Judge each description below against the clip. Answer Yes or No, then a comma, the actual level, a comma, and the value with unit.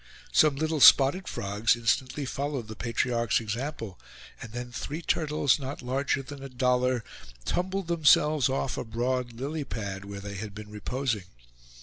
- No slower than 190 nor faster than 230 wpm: No, average, 150 wpm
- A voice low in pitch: Yes, low, 125 Hz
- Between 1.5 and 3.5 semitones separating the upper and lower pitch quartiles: No, average, 4.1 semitones